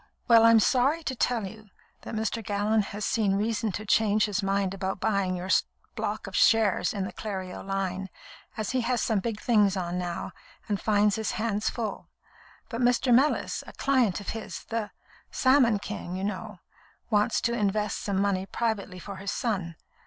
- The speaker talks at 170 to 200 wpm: Yes, average, 180 wpm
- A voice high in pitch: Yes, high, 210 Hz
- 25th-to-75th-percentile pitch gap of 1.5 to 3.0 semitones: Yes, narrow, 2.6 semitones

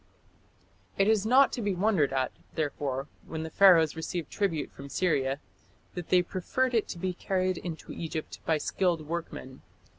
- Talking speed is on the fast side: No, average, 170 wpm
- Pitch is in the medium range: Yes, medium, 170 Hz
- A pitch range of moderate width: Yes, average, 3.9 semitones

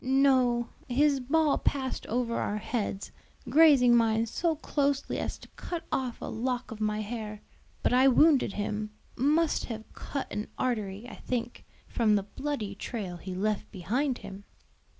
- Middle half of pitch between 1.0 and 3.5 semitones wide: No, average, 4.3 semitones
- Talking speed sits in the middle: Yes, average, 155 wpm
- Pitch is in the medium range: No, high, 240 Hz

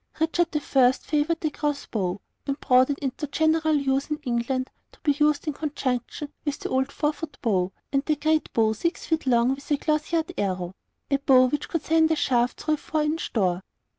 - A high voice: Yes, very high, 285 Hz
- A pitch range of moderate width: Yes, average, 3.4 semitones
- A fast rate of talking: Yes, fast, 210 wpm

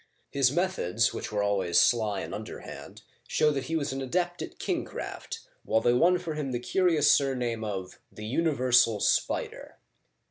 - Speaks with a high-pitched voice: No, low, 130 Hz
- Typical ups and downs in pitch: No, wide, 6.0 semitones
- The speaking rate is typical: Yes, average, 165 wpm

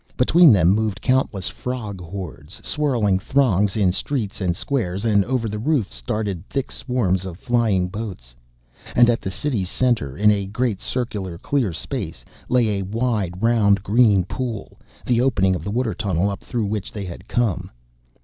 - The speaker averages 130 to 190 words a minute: Yes, average, 170 wpm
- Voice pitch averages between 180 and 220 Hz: No, low, 105 Hz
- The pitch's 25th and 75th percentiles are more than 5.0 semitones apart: No, average, 4.4 semitones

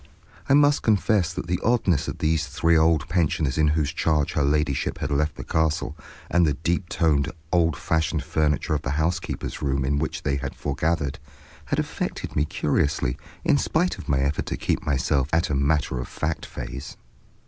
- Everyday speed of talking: Yes, average, 180 wpm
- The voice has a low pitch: Yes, very low, 75 Hz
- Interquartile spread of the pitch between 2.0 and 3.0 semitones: Yes, average, 2.7 semitones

